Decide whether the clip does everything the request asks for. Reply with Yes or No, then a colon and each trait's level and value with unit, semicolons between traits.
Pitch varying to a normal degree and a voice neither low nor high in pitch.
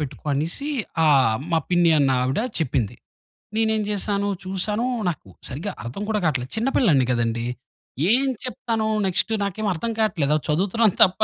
No: wide, 7.7 semitones; medium, 180 Hz